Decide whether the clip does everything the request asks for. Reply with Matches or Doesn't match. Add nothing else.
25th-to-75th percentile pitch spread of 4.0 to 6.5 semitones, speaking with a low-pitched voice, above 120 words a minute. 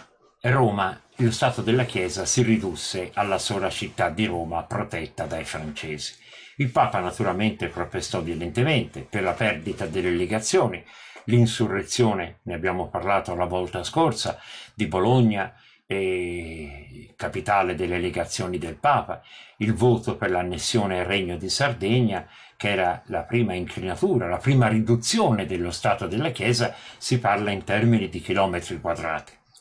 Matches